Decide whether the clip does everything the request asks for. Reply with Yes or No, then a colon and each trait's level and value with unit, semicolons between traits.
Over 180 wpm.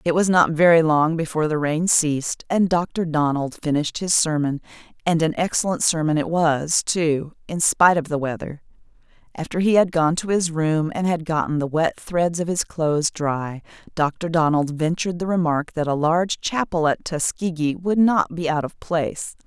Yes: average, 190 wpm